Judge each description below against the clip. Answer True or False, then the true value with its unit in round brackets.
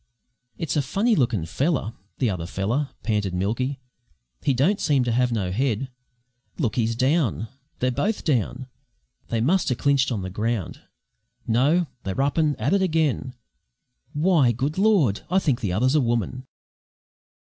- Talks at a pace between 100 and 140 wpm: False (155 wpm)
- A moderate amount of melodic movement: True (4.9 semitones)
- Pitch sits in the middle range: False (130 Hz)